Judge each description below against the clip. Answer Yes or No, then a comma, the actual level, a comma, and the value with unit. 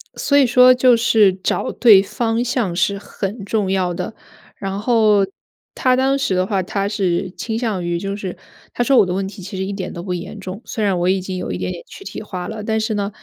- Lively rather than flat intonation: No, average, 3.4 semitones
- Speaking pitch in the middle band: No, high, 200 Hz